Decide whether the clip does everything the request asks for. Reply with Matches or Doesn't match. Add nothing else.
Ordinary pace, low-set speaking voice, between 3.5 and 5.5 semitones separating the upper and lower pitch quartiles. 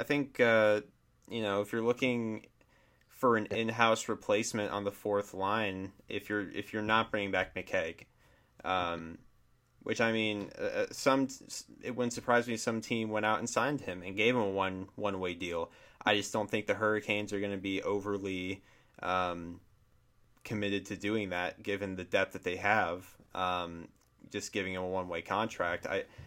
Doesn't match